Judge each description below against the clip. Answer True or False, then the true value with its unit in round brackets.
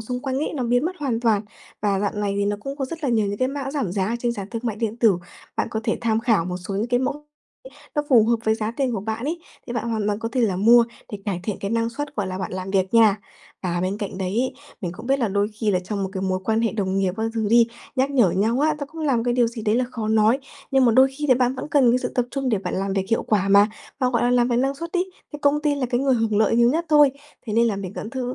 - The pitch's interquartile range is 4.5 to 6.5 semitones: False (4.1 semitones)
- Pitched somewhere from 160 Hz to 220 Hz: False (230 Hz)